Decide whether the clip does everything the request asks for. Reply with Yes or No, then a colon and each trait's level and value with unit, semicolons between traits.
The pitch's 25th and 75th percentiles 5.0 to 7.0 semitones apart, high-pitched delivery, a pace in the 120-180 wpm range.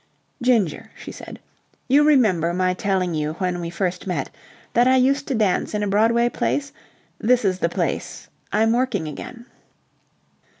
Yes: wide, 5.4 semitones; high, 210 Hz; average, 160 wpm